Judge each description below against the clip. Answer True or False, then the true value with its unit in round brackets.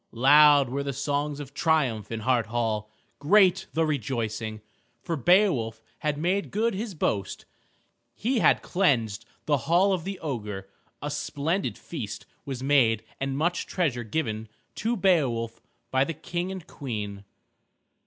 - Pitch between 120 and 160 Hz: True (140 Hz)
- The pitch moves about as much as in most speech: False (7.0 semitones)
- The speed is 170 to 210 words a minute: False (145 wpm)